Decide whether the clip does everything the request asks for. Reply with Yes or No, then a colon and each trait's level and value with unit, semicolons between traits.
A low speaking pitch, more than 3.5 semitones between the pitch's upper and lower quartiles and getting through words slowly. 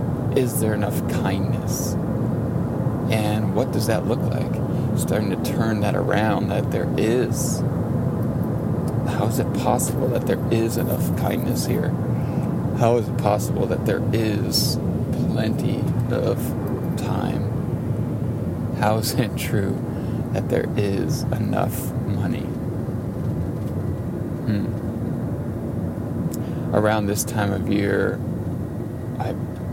No: low, 115 Hz; average, 3.1 semitones; slow, 110 wpm